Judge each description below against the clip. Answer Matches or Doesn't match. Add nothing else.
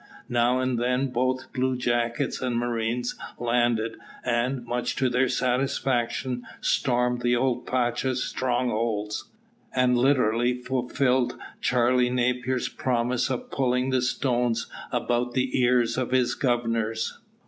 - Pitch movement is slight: Matches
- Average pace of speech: Doesn't match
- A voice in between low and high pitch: Doesn't match